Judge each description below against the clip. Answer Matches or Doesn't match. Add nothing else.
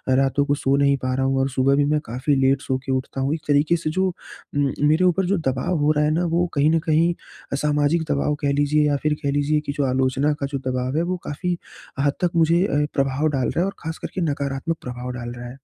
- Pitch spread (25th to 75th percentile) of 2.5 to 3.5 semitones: Matches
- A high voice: Doesn't match